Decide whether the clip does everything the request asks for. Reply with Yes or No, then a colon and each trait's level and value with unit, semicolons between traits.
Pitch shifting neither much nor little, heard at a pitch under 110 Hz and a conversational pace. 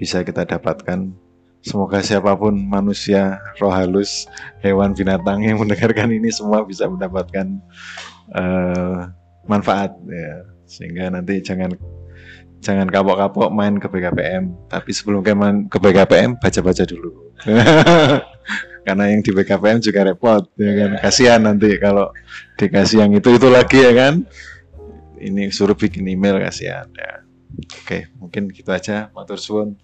No: narrow, 2.3 semitones; low, 100 Hz; average, 130 wpm